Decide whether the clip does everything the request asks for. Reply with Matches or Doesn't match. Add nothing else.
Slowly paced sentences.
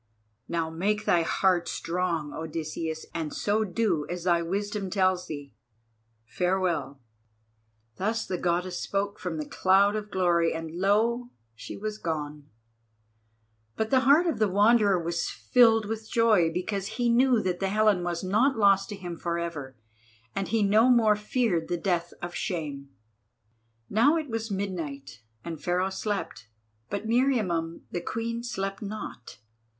Doesn't match